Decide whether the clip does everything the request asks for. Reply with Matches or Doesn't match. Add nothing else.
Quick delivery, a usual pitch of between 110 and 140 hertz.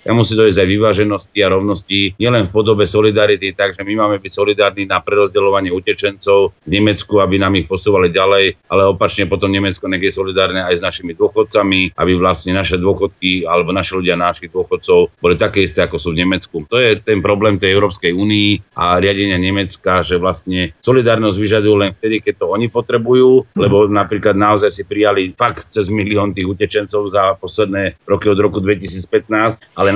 Doesn't match